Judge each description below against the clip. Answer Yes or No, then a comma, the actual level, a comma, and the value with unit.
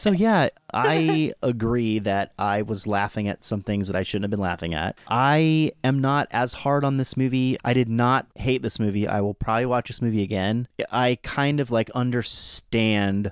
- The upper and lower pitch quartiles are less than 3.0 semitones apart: No, average, 4.1 semitones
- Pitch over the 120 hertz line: No, low, 115 Hz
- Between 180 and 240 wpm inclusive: Yes, average, 200 wpm